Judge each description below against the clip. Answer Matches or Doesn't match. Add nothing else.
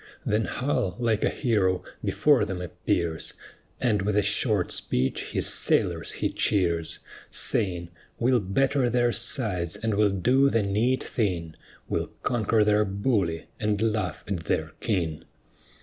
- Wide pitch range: Doesn't match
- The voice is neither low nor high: Doesn't match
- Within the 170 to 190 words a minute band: Doesn't match